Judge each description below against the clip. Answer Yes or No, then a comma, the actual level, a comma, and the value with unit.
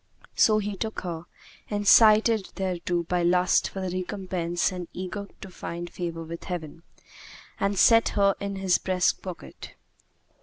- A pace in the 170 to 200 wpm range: No, average, 140 wpm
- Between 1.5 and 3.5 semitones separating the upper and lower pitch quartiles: Yes, narrow, 2.5 semitones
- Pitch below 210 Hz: Yes, medium, 185 Hz